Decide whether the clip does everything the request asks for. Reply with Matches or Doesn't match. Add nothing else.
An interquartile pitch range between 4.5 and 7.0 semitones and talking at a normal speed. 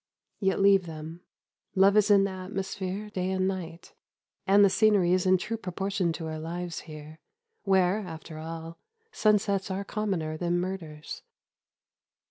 Doesn't match